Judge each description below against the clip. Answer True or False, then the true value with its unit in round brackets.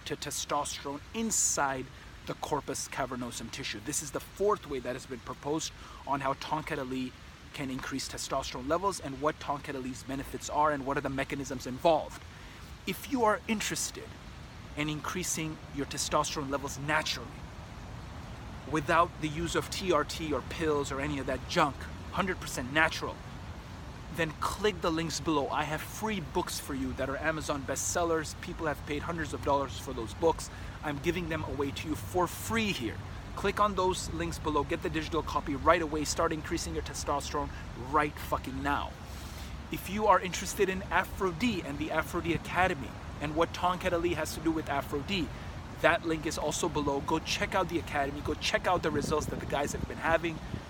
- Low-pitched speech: False (150 Hz)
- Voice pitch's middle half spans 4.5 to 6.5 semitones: False (3.6 semitones)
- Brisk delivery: False (175 wpm)